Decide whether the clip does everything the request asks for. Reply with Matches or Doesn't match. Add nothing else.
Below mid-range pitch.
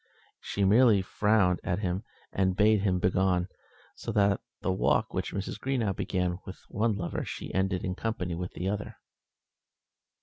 Matches